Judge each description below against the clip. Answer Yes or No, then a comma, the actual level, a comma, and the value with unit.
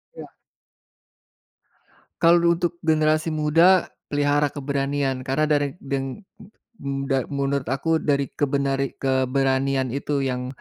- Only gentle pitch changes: Yes, narrow, 2.2 semitones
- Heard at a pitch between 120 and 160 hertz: Yes, medium, 140 Hz